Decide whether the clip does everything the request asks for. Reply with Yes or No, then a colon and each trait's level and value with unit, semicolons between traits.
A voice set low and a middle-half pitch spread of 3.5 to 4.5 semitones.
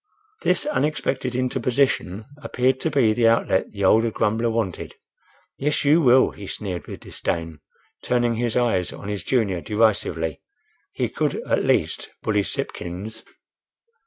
Yes: low, 115 Hz; average, 4.2 semitones